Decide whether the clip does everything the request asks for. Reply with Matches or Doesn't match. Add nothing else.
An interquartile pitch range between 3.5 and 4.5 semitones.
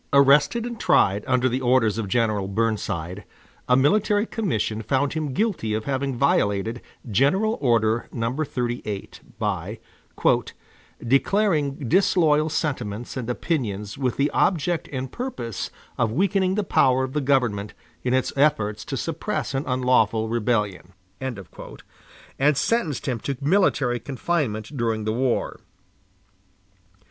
Doesn't match